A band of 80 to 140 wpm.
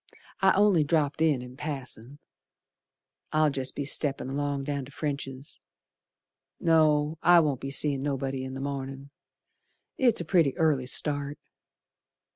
Yes: slow, 135 wpm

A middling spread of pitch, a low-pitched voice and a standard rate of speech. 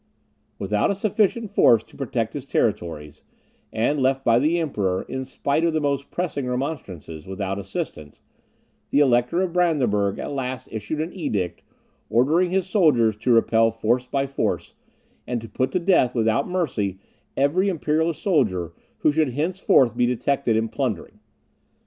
No: wide, 6.3 semitones; low, 130 Hz; average, 155 wpm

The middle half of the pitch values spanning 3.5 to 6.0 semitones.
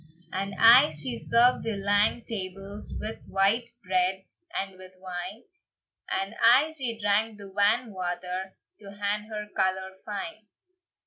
No: average, 2.7 semitones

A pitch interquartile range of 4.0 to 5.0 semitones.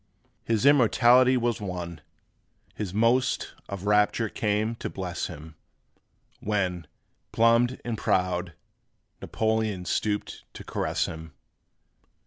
Yes: average, 4.3 semitones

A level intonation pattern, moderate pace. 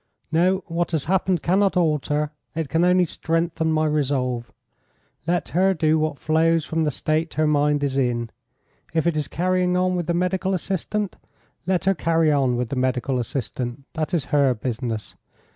No: average, 4.0 semitones; average, 175 wpm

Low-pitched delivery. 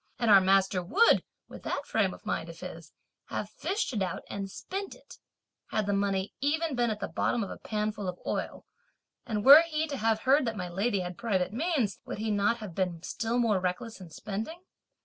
No: high, 215 Hz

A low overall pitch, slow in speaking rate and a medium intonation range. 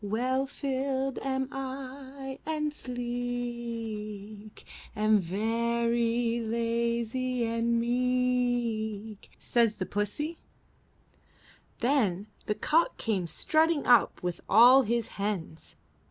No: high, 235 Hz; slow, 90 wpm; average, 3.2 semitones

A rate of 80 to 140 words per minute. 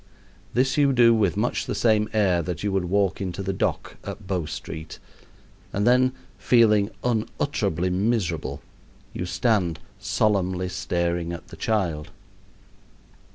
Yes: slow, 135 wpm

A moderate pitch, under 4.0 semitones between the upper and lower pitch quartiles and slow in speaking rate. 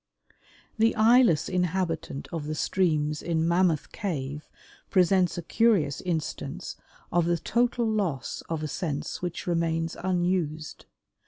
Yes: medium, 170 Hz; average, 3.2 semitones; slow, 120 wpm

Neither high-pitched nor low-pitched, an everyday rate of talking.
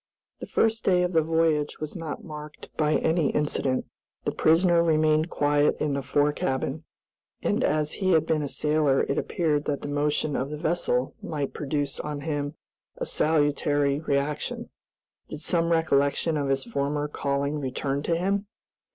Yes: medium, 150 Hz; average, 165 wpm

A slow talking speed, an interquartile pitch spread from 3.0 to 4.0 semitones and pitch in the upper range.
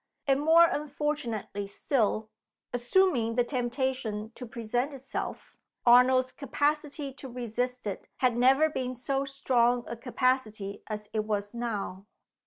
Yes: slow, 125 wpm; average, 3.4 semitones; very high, 250 Hz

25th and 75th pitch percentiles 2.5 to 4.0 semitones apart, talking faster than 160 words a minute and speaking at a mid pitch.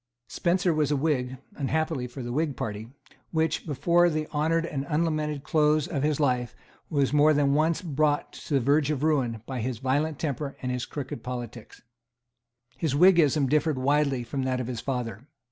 Yes: average, 3.2 semitones; average, 180 wpm; medium, 145 Hz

